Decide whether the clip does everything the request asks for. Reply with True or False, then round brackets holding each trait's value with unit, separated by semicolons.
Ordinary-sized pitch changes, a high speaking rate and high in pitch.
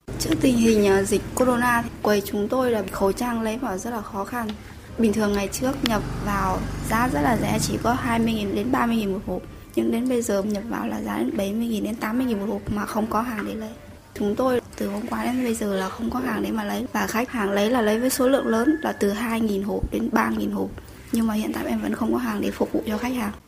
True (3.1 semitones; 260 wpm; 220 Hz)